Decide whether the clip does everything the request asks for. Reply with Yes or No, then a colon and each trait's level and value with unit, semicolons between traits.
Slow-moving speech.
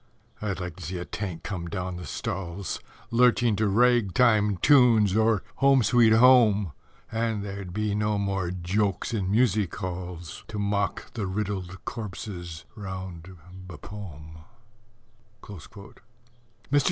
Yes: slow, 130 wpm